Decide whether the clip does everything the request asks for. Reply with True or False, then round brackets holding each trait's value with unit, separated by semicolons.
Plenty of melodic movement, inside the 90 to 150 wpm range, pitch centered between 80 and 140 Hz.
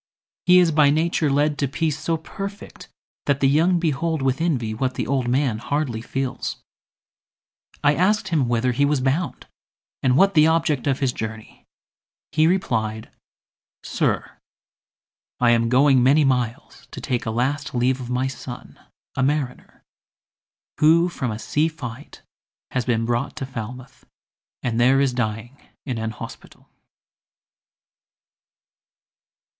False (3.9 semitones; 140 wpm; 135 Hz)